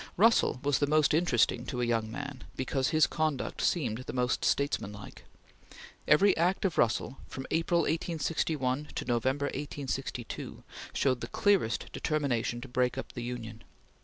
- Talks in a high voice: No, low, 135 Hz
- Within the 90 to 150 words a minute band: Yes, average, 145 wpm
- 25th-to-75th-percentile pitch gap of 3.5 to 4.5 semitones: Yes, average, 4.1 semitones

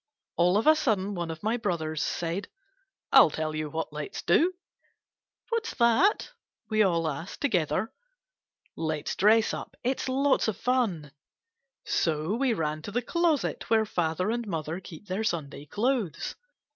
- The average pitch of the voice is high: Yes, high, 195 Hz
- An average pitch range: No, wide, 6.8 semitones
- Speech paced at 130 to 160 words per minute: No, average, 170 wpm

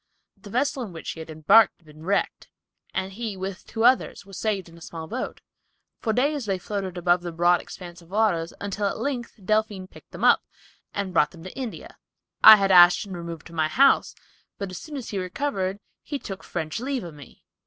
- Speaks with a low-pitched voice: No, high, 190 Hz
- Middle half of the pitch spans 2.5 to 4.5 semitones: Yes, average, 4.2 semitones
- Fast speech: Yes, fast, 215 wpm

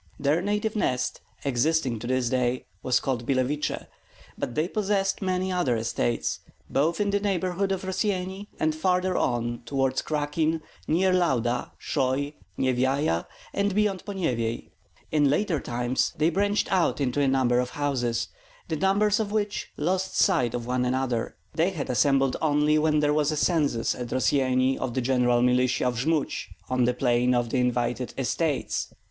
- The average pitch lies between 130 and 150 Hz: Yes, medium, 140 Hz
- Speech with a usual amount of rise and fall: No, wide, 6.4 semitones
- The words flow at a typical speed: Yes, average, 160 wpm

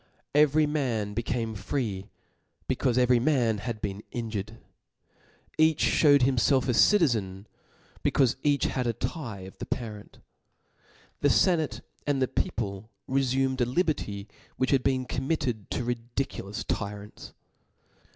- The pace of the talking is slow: Yes, slow, 130 wpm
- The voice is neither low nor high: No, low, 125 Hz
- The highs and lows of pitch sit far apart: No, average, 4.3 semitones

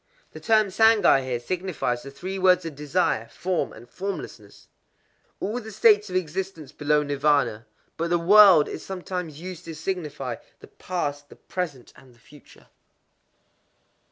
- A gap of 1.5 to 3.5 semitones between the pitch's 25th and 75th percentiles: No, average, 4.8 semitones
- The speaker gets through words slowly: No, average, 145 wpm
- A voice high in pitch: No, medium, 170 Hz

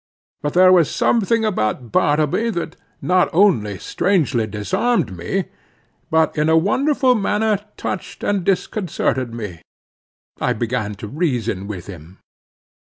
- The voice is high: No, medium, 155 Hz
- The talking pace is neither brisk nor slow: No, slow, 125 wpm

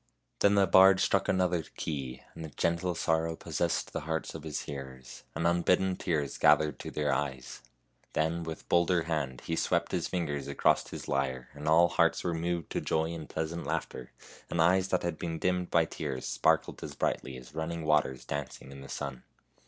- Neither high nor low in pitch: No, very low, 80 Hz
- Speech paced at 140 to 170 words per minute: No, average, 190 wpm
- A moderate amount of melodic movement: Yes, average, 3.3 semitones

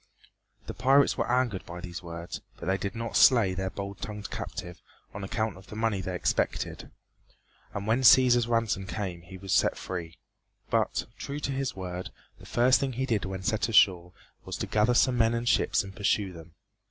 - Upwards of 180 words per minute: Yes, average, 195 wpm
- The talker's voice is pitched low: Yes, low, 100 Hz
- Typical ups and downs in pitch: Yes, average, 4.2 semitones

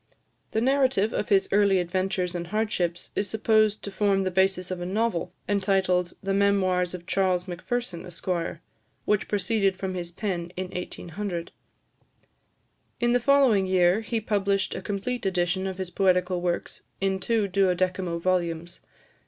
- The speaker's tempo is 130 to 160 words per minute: Yes, average, 150 wpm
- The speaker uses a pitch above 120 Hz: Yes, high, 190 Hz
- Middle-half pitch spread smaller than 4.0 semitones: Yes, narrow, 2.4 semitones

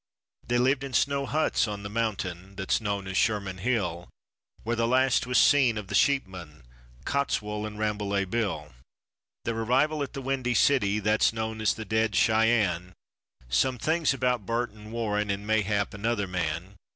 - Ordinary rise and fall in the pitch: Yes, average, 3.6 semitones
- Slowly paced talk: No, average, 165 wpm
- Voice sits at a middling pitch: No, low, 110 Hz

